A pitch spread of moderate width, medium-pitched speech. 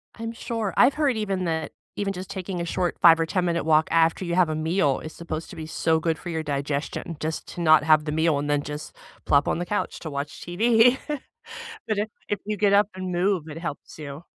Yes: average, 3.7 semitones; medium, 170 Hz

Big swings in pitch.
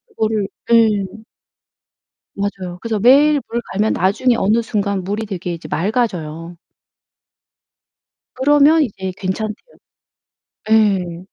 No: average, 3.6 semitones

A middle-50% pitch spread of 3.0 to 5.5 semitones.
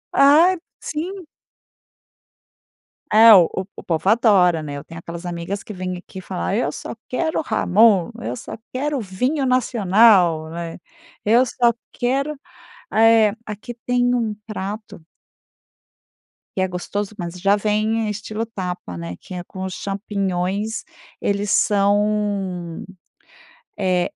Yes: average, 4.0 semitones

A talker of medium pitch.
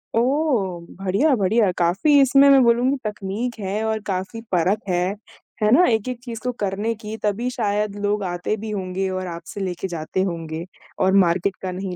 No: high, 205 Hz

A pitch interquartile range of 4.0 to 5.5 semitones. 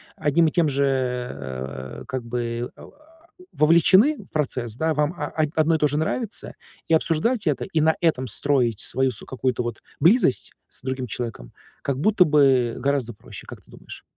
Yes: average, 4.5 semitones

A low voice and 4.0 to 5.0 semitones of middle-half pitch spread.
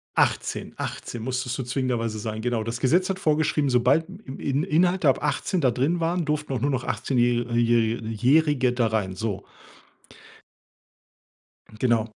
Yes: low, 125 Hz; average, 4.4 semitones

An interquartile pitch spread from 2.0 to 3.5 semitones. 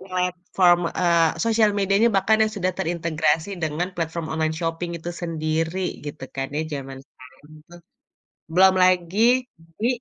Yes: average, 2.7 semitones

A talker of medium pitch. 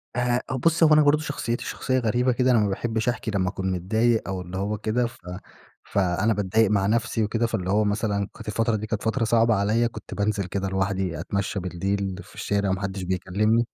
No: low, 105 Hz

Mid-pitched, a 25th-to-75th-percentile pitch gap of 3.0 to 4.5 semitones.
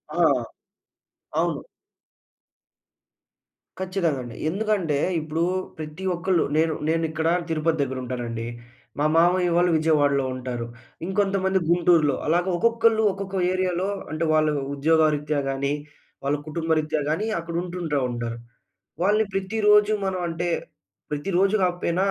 Yes: medium, 165 Hz; average, 3.9 semitones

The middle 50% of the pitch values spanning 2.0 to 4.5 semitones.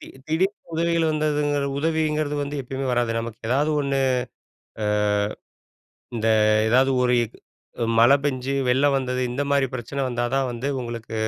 Yes: average, 3.3 semitones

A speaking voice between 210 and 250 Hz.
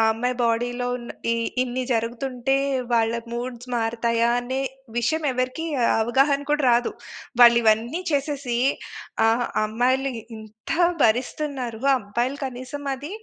Yes: high, 245 Hz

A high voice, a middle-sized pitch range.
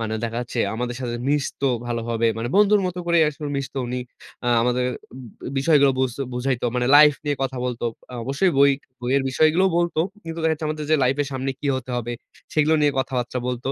No: low, 135 Hz; average, 3.8 semitones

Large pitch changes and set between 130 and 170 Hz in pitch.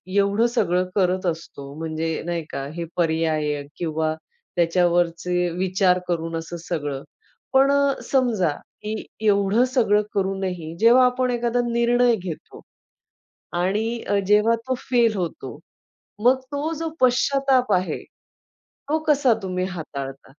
No: wide, 6.2 semitones; high, 190 Hz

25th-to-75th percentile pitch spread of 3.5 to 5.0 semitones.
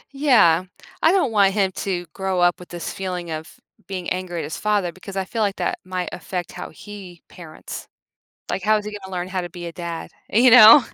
No: average, 2.8 semitones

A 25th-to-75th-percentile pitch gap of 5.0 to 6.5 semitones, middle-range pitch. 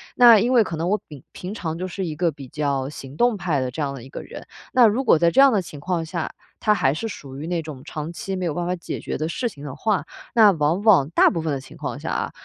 Yes: wide, 5.4 semitones; medium, 165 Hz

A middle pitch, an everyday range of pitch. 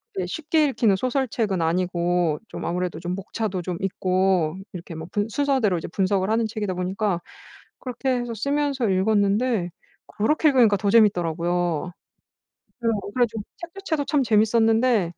No: high, 205 Hz; average, 5.0 semitones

